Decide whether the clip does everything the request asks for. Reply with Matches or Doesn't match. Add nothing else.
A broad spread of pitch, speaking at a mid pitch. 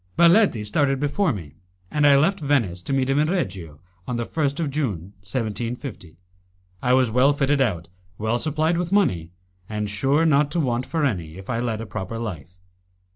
Doesn't match